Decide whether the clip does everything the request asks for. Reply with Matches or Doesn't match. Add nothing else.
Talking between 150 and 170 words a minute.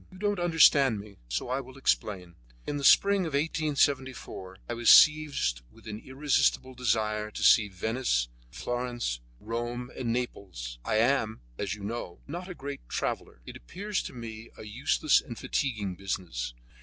Matches